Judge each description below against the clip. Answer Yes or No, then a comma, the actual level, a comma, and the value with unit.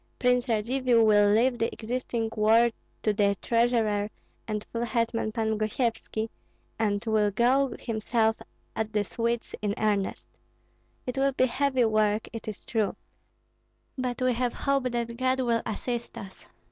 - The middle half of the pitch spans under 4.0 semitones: Yes, narrow, 2.4 semitones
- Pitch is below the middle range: No, high, 230 Hz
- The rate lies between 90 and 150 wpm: Yes, average, 145 wpm